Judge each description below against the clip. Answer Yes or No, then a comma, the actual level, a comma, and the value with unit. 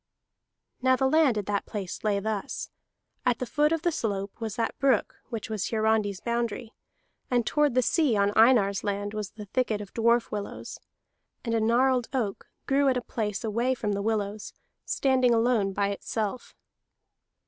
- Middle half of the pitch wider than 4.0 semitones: No, average, 3.6 semitones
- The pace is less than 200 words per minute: Yes, average, 170 wpm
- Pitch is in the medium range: No, high, 225 Hz